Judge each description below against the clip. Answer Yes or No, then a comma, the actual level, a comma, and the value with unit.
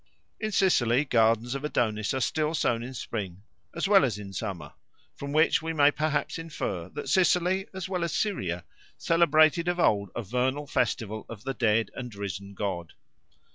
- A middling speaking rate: Yes, average, 175 wpm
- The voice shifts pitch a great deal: Yes, wide, 7.5 semitones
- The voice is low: Yes, low, 125 Hz